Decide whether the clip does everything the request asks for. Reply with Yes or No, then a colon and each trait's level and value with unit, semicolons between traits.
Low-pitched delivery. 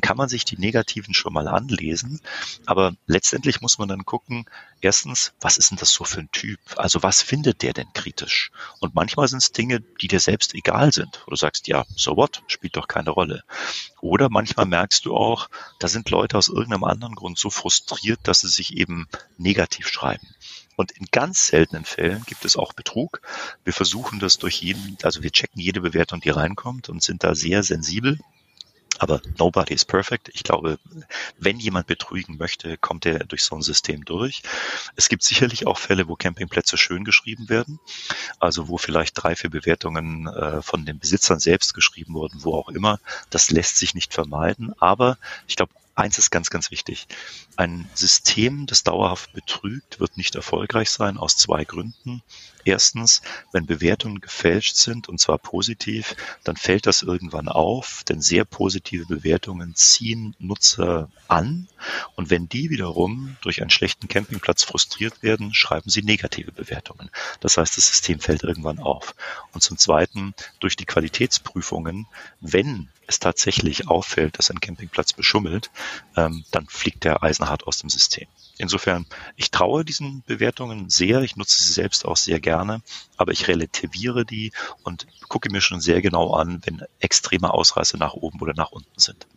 Yes: very low, 95 Hz